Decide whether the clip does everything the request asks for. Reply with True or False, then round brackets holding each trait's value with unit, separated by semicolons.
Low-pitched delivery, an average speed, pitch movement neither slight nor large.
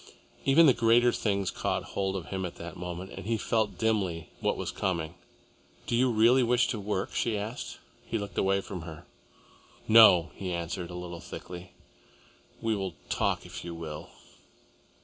True (95 Hz; 170 wpm; 4.3 semitones)